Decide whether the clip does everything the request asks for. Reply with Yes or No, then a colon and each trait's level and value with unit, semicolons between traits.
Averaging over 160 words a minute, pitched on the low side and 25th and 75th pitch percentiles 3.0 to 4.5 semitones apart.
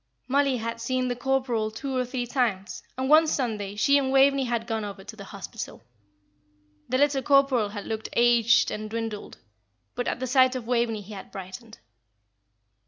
No: average, 175 wpm; high, 240 Hz; average, 3.4 semitones